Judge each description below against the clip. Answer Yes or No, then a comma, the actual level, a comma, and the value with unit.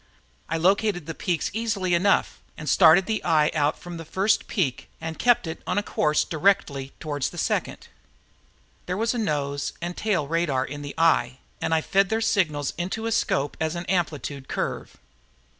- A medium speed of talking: Yes, average, 180 wpm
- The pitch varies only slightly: No, average, 4.7 semitones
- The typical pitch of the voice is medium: Yes, medium, 165 Hz